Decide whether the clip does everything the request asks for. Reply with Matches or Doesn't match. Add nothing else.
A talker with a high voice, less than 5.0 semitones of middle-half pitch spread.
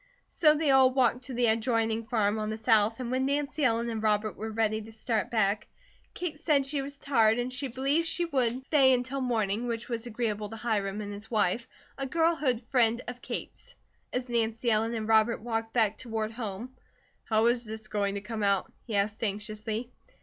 Matches